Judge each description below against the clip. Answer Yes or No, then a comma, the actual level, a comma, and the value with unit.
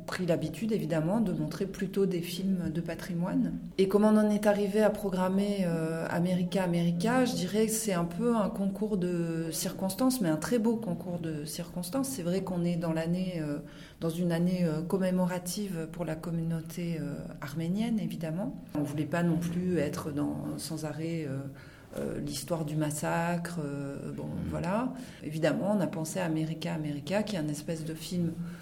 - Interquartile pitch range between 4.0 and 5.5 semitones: No, average, 3.2 semitones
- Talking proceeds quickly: No, average, 180 wpm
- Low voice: No, medium, 170 Hz